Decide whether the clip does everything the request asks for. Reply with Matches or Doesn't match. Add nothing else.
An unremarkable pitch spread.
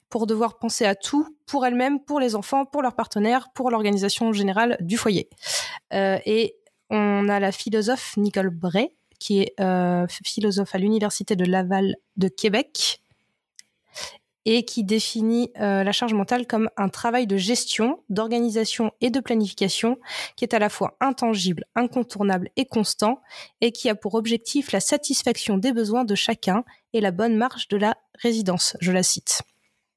Matches